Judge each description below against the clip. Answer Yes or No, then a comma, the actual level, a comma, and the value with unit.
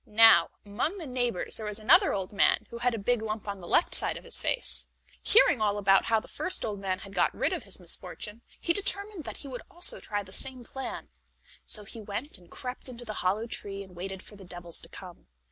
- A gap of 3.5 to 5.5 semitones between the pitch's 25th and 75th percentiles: Yes, average, 4.3 semitones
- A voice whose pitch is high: Yes, high, 215 Hz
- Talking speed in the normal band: No, fast, 235 wpm